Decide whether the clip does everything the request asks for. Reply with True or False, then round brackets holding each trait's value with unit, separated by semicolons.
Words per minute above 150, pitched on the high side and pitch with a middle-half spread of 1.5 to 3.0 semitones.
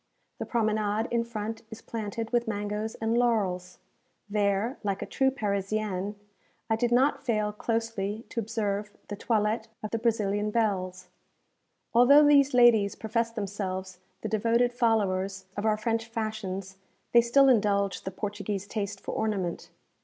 False (145 wpm; 215 Hz; 2.4 semitones)